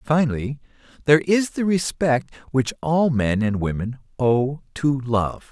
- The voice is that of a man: Yes, male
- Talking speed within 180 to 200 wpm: No, average, 150 wpm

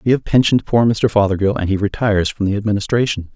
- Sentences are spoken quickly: Yes, fast, 215 wpm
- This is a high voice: No, low, 105 Hz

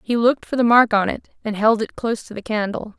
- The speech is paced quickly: Yes, fast, 280 wpm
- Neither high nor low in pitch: No, high, 220 Hz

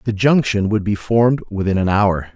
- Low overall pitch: Yes, low, 105 Hz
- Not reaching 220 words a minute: Yes, fast, 205 wpm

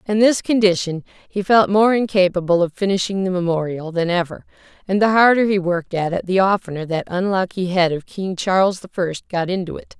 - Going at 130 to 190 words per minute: No, average, 200 wpm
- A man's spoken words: No, female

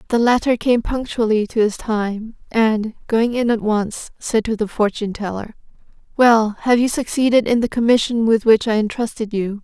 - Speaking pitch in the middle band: No, high, 225 Hz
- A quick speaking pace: No, average, 180 wpm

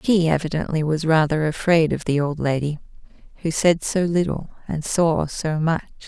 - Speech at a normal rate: Yes, average, 170 wpm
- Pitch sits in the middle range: Yes, medium, 160 Hz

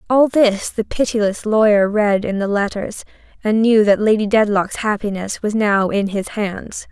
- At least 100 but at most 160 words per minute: No, average, 175 wpm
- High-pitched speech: Yes, high, 210 Hz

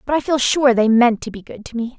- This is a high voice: Yes, high, 245 Hz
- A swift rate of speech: Yes, fast, 330 wpm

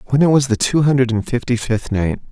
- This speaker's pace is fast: Yes, fast, 260 wpm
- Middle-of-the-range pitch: No, low, 125 Hz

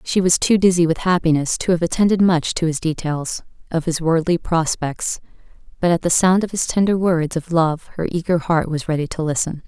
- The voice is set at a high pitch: No, medium, 170 Hz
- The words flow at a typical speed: No, fast, 210 wpm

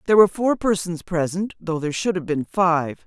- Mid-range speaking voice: Yes, medium, 175 Hz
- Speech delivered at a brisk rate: Yes, fast, 215 wpm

